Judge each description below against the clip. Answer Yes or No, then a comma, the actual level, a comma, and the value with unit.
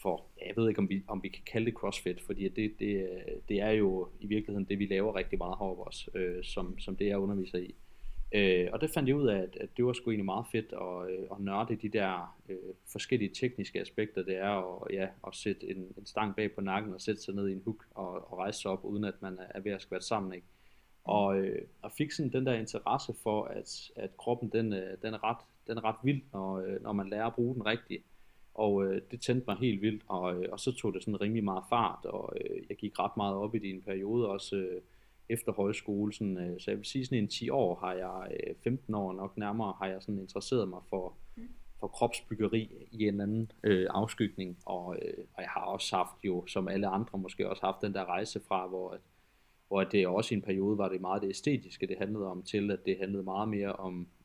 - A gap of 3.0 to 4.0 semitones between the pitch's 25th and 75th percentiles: No, narrow, 2.5 semitones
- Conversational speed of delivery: No, fast, 250 wpm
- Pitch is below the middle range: Yes, low, 100 Hz